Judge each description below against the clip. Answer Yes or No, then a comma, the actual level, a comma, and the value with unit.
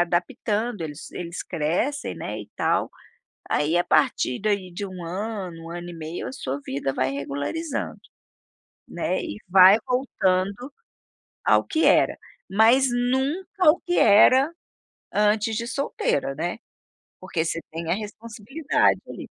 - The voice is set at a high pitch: Yes, high, 200 Hz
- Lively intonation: Yes, wide, 6.7 semitones